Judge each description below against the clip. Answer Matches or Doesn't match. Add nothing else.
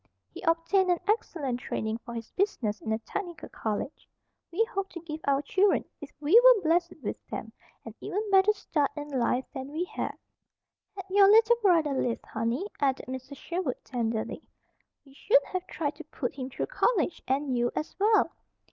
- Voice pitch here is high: Matches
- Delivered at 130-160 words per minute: Doesn't match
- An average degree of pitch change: Doesn't match